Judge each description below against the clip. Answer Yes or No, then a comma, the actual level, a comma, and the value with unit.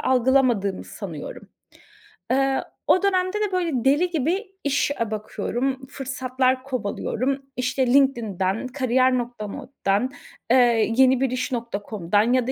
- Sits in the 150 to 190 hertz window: No, very high, 260 Hz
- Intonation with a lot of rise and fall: No, narrow, 2.4 semitones